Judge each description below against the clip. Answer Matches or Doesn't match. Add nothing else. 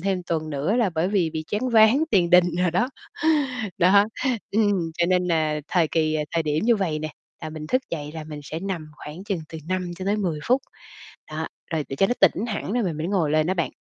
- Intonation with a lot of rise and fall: Doesn't match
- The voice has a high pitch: Doesn't match